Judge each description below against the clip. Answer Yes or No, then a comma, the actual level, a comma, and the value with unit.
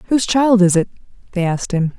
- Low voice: No, high, 200 Hz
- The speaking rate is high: Yes, fast, 210 wpm